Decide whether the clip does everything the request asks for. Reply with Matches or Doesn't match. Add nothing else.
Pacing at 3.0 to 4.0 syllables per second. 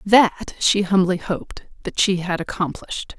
Doesn't match